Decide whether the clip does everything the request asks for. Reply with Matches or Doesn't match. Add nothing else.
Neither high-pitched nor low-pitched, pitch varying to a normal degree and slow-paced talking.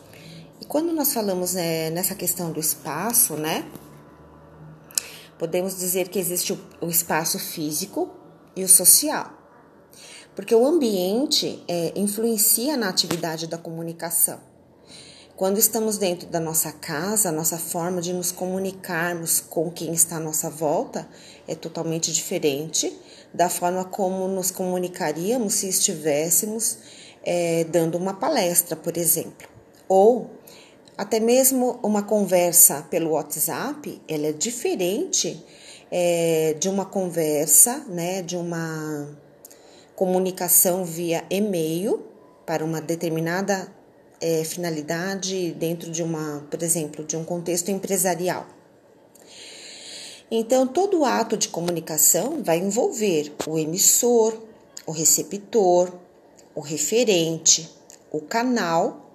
Matches